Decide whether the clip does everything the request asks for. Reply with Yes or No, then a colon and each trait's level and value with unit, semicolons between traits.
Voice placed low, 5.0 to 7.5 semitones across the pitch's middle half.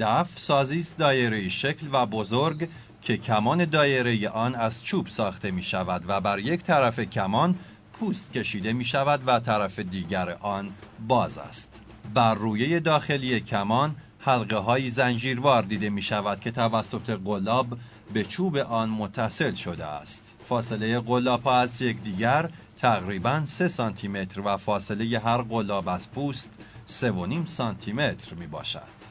No: low, 115 Hz; average, 3.8 semitones